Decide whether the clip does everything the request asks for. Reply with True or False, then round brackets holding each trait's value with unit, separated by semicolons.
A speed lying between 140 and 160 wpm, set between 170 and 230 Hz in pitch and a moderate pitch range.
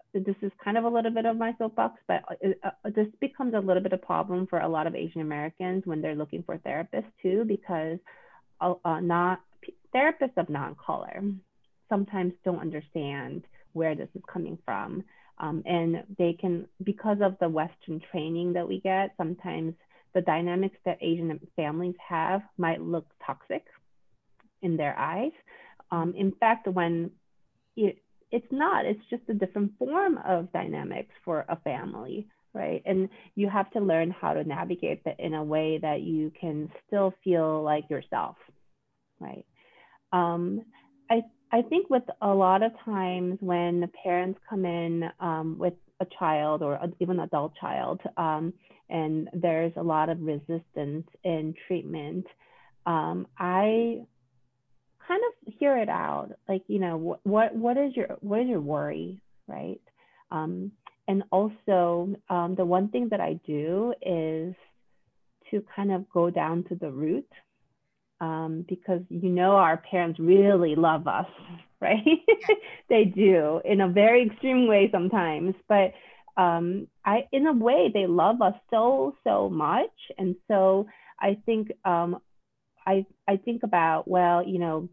True (155 wpm; 185 Hz; 4.0 semitones)